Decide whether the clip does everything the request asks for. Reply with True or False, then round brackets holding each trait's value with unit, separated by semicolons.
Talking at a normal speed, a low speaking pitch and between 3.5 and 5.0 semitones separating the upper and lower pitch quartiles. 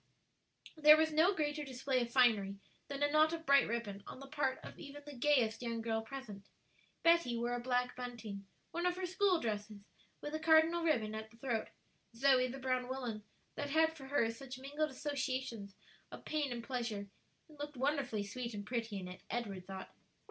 False (190 wpm; 255 Hz; 4.4 semitones)